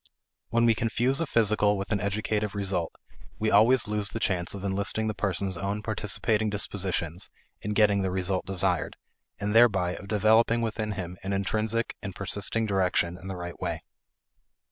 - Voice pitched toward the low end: Yes, low, 100 Hz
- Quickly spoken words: No, average, 165 wpm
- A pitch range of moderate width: No, narrow, 2.3 semitones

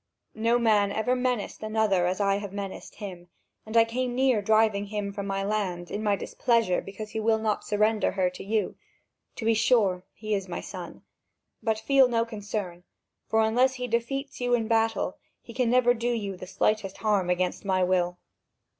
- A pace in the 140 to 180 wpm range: No, average, 190 wpm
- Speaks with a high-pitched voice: Yes, high, 215 Hz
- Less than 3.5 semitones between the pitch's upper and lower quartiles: Yes, average, 2.8 semitones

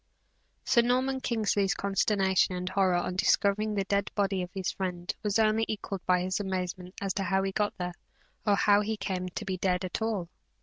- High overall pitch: Yes, high, 195 Hz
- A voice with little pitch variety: Yes, narrow, 2.2 semitones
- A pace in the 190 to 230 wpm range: Yes, average, 200 wpm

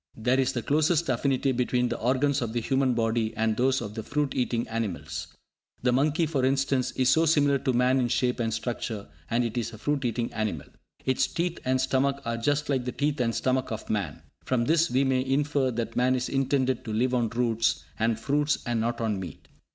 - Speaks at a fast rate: Yes, fast, 215 wpm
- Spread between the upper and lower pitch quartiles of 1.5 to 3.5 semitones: Yes, average, 2.8 semitones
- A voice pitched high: No, low, 125 Hz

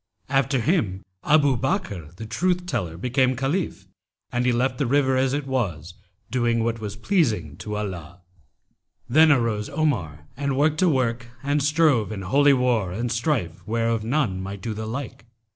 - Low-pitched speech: Yes, low, 120 Hz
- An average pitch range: Yes, average, 5.0 semitones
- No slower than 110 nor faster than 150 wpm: No, average, 170 wpm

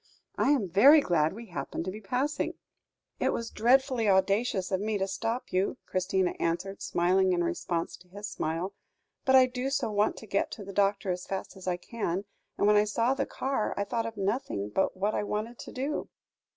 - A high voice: Yes, high, 205 Hz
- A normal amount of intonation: Yes, average, 3.8 semitones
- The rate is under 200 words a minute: No, fast, 205 wpm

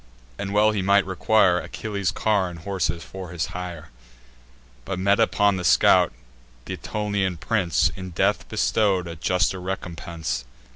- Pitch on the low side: Yes, very low, 95 Hz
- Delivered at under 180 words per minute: Yes, average, 145 wpm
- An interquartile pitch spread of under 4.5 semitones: Yes, average, 2.7 semitones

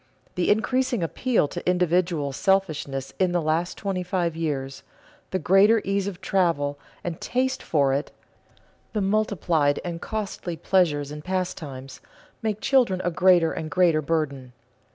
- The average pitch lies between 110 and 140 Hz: No, medium, 175 Hz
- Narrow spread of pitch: No, average, 4.2 semitones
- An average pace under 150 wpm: Yes, average, 140 wpm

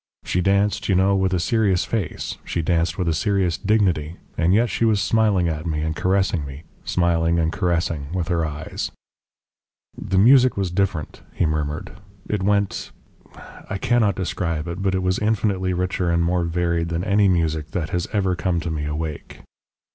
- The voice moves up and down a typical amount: Yes, average, 3.1 semitones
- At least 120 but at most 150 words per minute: No, average, 180 wpm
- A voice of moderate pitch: No, very low, 90 Hz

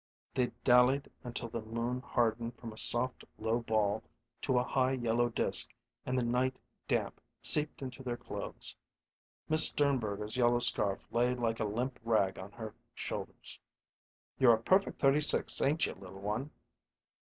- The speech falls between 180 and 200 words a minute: No, average, 155 wpm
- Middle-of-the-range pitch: No, low, 120 Hz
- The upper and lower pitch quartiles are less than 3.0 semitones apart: Yes, narrow, 2.5 semitones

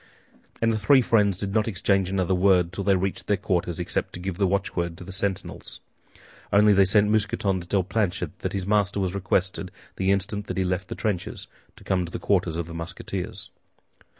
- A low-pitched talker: Yes, very low, 95 Hz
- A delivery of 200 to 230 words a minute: Yes, fast, 205 wpm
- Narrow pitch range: Yes, narrow, 2.0 semitones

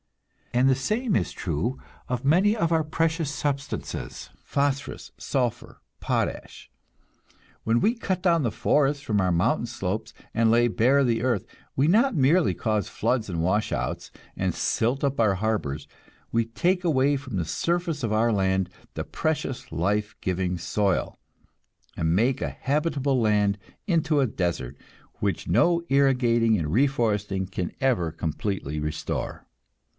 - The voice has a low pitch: Yes, low, 120 Hz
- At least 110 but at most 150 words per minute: Yes, average, 145 wpm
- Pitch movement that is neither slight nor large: No, wide, 6.1 semitones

